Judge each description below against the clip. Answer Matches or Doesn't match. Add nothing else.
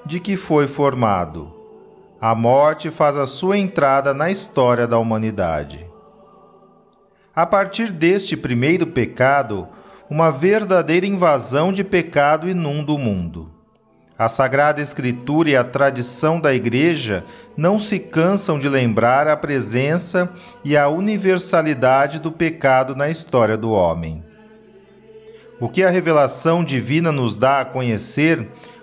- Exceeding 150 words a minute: Doesn't match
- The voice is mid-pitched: Matches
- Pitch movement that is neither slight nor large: Doesn't match